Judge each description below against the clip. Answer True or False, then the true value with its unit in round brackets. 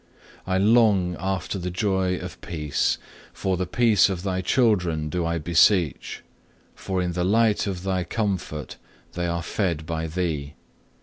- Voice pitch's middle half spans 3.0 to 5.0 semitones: False (2.5 semitones)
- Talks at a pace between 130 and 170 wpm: True (160 wpm)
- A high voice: False (90 Hz)